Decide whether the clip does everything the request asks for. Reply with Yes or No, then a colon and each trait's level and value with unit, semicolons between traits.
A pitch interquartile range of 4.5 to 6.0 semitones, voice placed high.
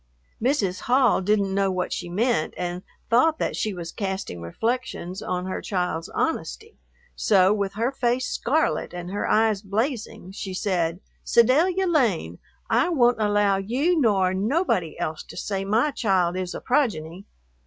Yes: average, 5.1 semitones; high, 200 Hz